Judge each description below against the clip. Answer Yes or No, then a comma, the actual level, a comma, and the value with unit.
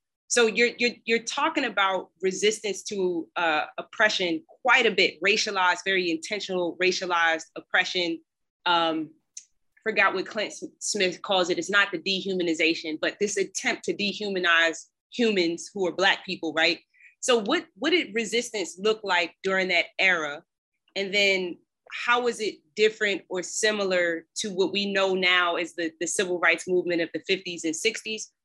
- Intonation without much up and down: No, average, 3.7 semitones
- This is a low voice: No, high, 190 Hz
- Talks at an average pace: Yes, average, 155 wpm